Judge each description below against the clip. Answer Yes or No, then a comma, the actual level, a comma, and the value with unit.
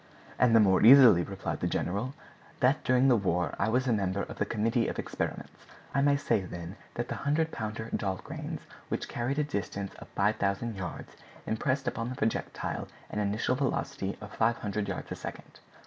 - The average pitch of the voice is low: Yes, low, 110 Hz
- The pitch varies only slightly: No, average, 4.3 semitones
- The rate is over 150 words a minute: Yes, average, 180 wpm